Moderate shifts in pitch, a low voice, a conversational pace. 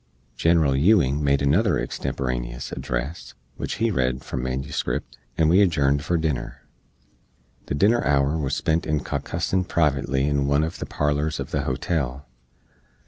Yes: average, 3.5 semitones; very low, 70 Hz; average, 145 wpm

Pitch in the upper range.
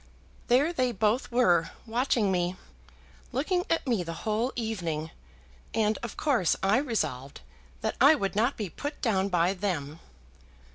Yes: high, 215 Hz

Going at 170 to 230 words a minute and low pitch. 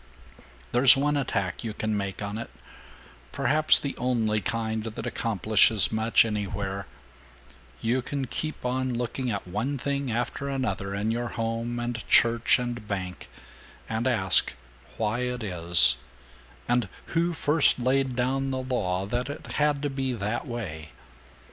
No: average, 145 wpm; low, 120 Hz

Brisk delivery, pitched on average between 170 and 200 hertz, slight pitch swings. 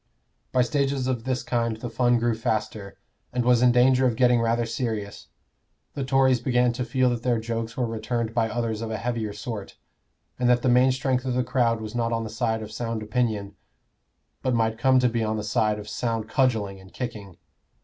No: fast, 210 wpm; low, 120 Hz; narrow, 2.0 semitones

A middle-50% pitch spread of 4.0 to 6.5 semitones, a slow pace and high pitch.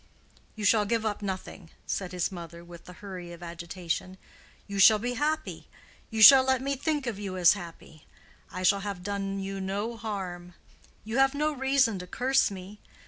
No: average, 4.4 semitones; average, 185 wpm; high, 200 Hz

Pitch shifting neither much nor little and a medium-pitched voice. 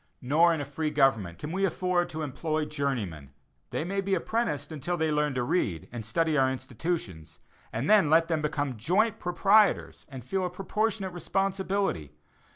No: wide, 5.7 semitones; medium, 155 Hz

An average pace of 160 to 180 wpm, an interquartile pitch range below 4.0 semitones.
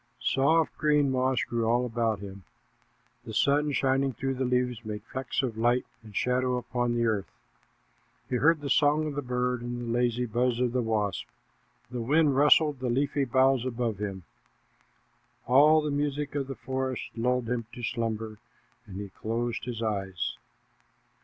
Yes: average, 165 wpm; average, 2.9 semitones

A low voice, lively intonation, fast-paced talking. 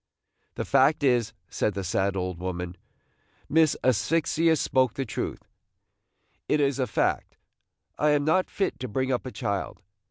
No: low, 130 Hz; wide, 6.5 semitones; average, 155 wpm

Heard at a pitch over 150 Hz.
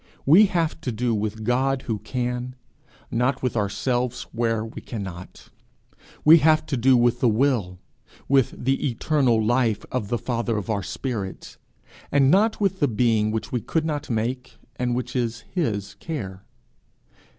No: low, 125 Hz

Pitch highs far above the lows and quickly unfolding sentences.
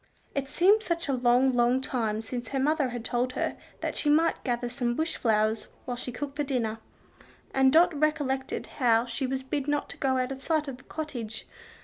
No: average, 3.3 semitones; fast, 210 wpm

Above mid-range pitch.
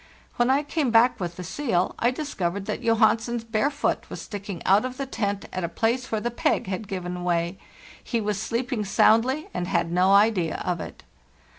Yes: high, 215 Hz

